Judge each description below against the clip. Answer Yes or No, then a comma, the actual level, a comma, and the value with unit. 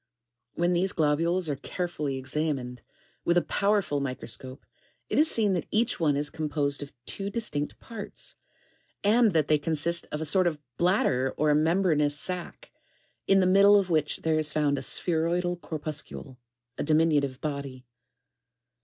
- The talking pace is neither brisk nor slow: Yes, average, 160 wpm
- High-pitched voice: No, medium, 155 Hz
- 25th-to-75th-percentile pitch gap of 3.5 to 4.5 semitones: Yes, average, 3.9 semitones